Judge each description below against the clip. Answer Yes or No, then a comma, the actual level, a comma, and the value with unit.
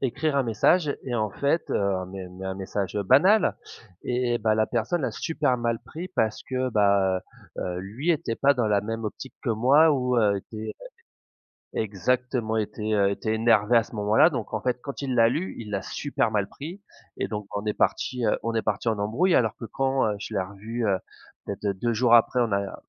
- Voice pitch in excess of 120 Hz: No, low, 115 Hz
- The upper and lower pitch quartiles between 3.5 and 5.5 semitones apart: Yes, average, 3.8 semitones